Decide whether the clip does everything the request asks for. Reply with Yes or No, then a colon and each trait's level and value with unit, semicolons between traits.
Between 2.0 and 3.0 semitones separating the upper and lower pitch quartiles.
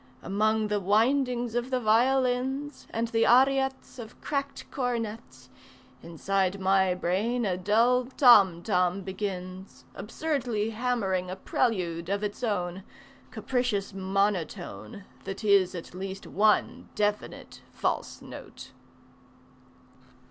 No: average, 4.5 semitones